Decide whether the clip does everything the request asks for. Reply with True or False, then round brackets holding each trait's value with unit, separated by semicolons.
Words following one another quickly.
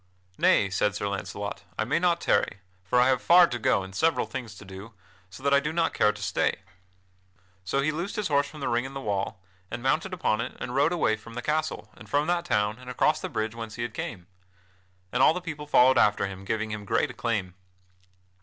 True (230 wpm)